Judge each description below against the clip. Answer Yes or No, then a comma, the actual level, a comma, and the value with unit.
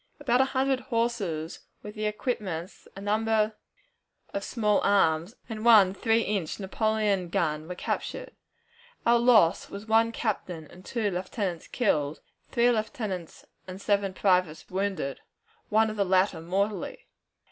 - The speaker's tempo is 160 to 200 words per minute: No, slow, 135 wpm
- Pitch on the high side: Yes, high, 205 Hz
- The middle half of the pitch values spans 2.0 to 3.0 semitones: No, average, 3.5 semitones